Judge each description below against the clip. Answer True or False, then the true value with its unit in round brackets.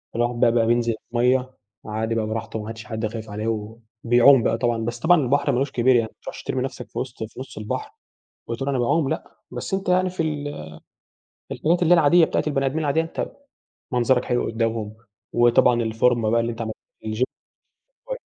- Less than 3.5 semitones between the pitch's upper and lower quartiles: False (3.8 semitones)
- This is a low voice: True (120 Hz)